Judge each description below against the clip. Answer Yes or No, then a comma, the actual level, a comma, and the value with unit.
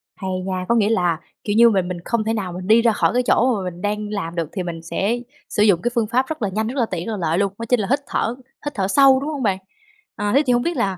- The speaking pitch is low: No, high, 210 Hz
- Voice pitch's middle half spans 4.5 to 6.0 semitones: No, average, 4.1 semitones